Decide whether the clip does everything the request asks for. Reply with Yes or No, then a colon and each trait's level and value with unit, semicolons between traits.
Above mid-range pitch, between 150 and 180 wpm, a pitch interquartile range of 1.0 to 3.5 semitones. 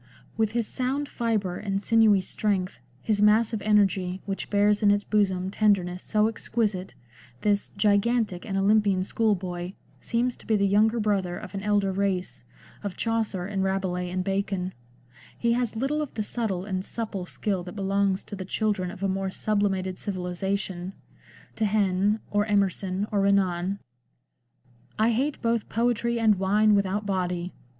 Yes: high, 200 Hz; average, 160 wpm; narrow, 2.4 semitones